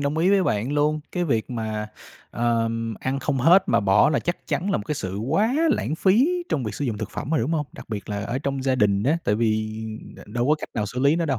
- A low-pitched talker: Yes, low, 130 Hz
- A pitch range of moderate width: No, wide, 6.4 semitones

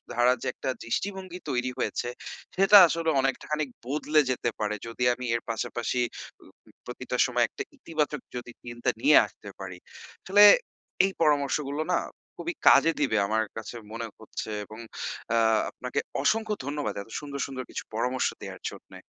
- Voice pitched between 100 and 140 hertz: Yes, low, 135 Hz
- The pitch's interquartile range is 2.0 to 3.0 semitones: No, average, 4.4 semitones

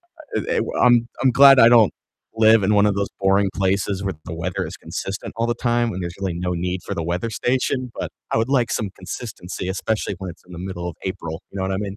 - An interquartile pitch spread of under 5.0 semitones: Yes, average, 3.9 semitones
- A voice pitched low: Yes, low, 100 Hz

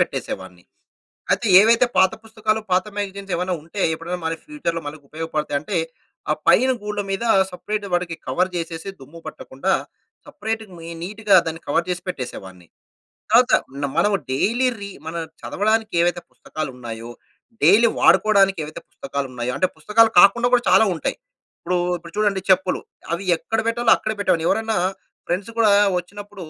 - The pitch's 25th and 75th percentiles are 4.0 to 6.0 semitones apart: Yes, average, 4.7 semitones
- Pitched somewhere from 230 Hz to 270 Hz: No, medium, 185 Hz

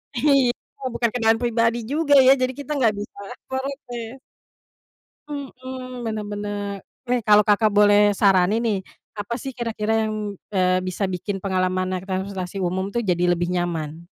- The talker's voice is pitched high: Yes, high, 210 Hz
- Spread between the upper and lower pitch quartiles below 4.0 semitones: No, average, 4.3 semitones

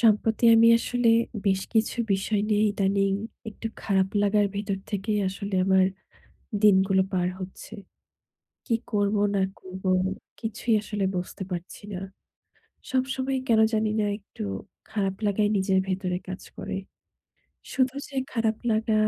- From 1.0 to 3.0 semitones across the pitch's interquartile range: Yes, narrow, 2.5 semitones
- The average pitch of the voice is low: No, high, 205 Hz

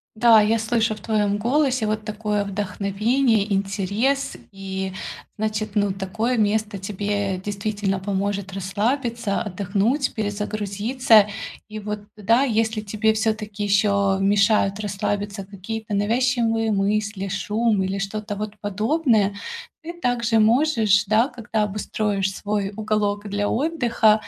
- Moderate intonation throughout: No, narrow, 1.9 semitones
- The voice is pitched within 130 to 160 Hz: No, high, 210 Hz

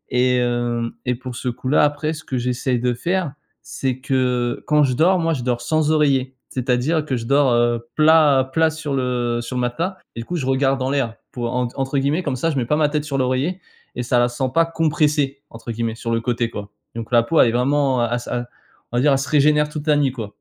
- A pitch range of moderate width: Yes, average, 3.6 semitones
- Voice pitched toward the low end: Yes, low, 130 Hz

